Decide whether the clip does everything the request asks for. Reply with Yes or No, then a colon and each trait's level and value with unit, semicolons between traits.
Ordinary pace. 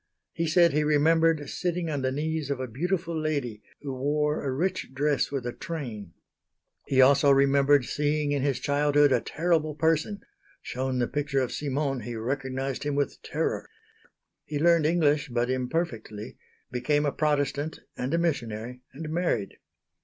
Yes: average, 160 wpm